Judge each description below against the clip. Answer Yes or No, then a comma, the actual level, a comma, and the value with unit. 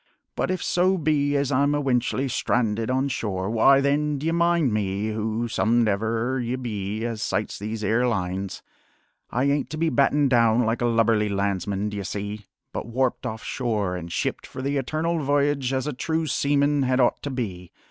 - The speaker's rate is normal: Yes, average, 180 wpm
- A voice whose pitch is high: No, low, 120 Hz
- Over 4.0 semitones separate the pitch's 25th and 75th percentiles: Yes, average, 4.8 semitones